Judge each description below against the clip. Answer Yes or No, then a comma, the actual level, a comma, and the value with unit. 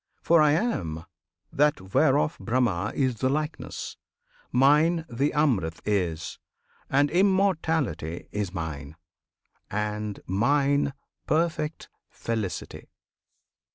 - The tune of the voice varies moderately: No, wide, 7.6 semitones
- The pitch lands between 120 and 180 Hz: Yes, low, 135 Hz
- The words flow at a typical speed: No, slow, 90 wpm